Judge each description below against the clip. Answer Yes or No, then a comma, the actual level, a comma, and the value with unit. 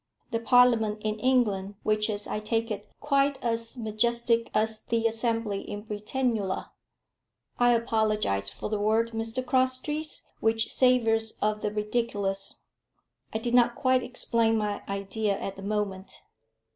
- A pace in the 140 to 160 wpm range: Yes, average, 145 wpm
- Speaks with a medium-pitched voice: No, high, 225 Hz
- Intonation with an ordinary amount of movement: No, narrow, 2.2 semitones